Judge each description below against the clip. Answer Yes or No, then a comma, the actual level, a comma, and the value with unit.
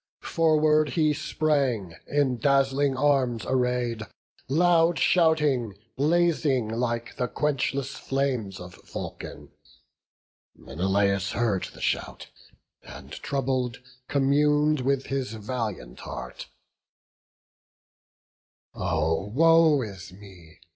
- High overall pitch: No, low, 130 Hz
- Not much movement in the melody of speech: No, wide, 5.6 semitones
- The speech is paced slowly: Yes, slow, 90 wpm